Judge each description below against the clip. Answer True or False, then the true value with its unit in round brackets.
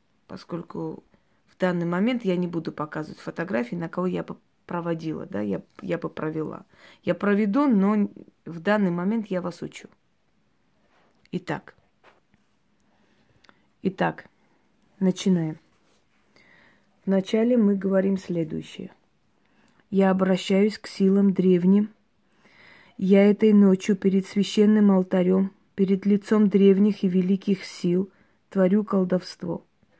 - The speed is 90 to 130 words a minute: True (110 wpm)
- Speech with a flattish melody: True (2.1 semitones)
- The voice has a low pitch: False (195 Hz)